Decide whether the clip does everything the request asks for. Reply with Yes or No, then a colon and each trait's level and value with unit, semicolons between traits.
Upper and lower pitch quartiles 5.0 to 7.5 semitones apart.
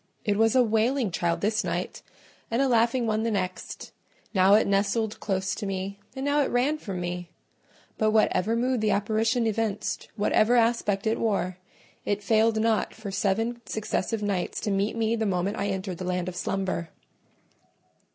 No: average, 2.8 semitones